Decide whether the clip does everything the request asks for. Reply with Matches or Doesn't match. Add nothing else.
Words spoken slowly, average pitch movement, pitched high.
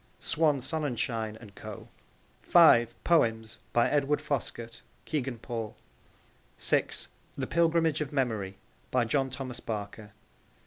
Doesn't match